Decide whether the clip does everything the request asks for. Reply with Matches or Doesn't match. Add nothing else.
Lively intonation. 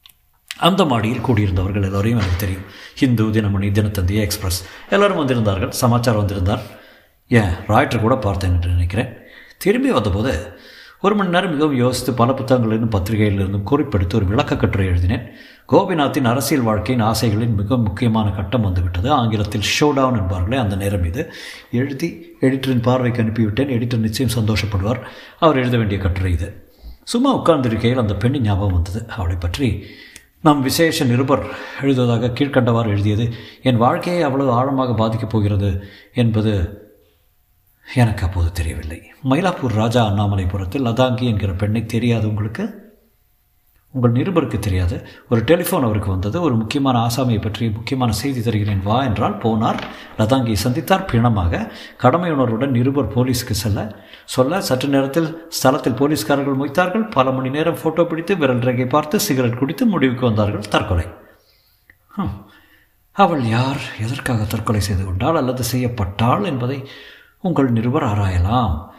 Doesn't match